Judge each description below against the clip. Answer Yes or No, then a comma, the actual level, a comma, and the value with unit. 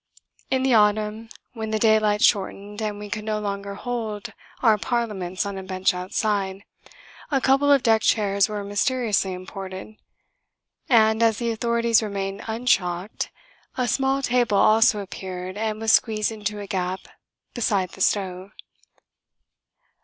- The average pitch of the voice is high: Yes, high, 210 Hz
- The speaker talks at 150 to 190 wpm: No, average, 140 wpm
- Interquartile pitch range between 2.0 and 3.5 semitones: Yes, narrow, 2.4 semitones